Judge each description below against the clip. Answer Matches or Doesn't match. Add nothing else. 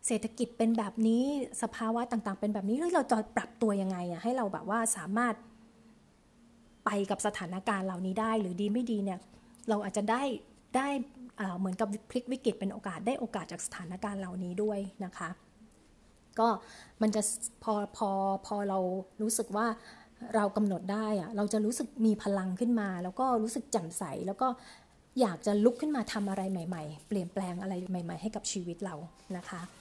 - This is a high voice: Matches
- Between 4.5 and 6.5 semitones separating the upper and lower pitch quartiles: Doesn't match